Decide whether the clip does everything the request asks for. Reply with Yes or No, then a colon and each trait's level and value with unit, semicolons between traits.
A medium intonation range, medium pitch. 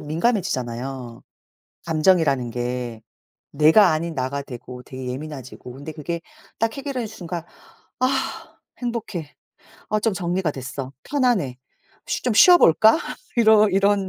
No: wide, 8.4 semitones; medium, 160 Hz